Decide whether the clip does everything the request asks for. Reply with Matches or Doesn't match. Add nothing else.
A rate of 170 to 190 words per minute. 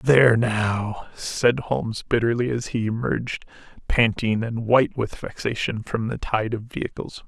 Doesn't match